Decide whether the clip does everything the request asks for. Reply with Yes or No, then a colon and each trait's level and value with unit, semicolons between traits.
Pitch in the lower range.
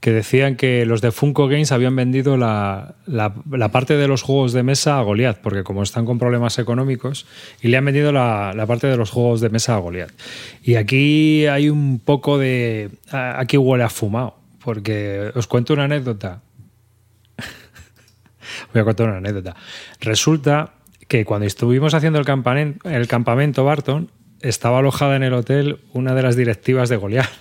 Yes: low, 125 Hz